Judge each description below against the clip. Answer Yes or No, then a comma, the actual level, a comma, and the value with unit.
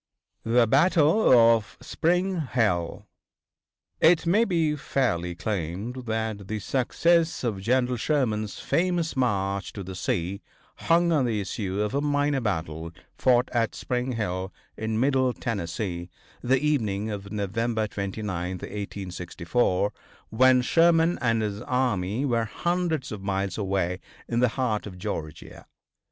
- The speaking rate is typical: No, slow, 130 wpm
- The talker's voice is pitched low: Yes, low, 115 Hz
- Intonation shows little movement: No, wide, 5.4 semitones